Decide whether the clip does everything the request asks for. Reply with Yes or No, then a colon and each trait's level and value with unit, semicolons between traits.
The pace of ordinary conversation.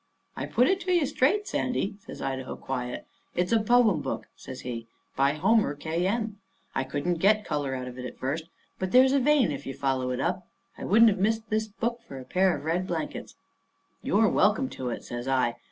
No: fast, 215 wpm